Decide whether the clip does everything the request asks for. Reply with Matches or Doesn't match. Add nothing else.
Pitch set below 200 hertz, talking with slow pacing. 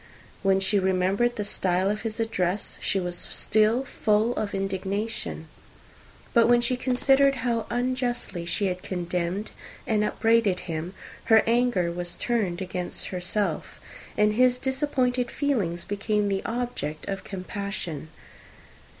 Doesn't match